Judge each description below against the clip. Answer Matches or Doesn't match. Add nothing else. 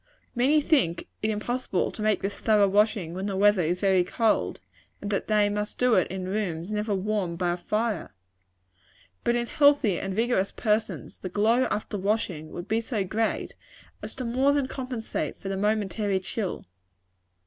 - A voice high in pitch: Matches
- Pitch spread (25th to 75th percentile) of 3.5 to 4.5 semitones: Doesn't match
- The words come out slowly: Doesn't match